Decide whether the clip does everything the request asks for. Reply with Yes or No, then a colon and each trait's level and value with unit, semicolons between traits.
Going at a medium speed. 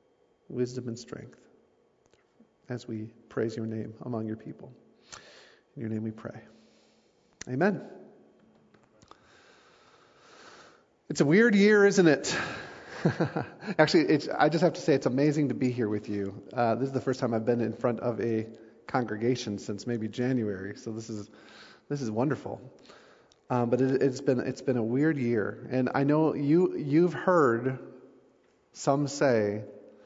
Yes: average, 155 wpm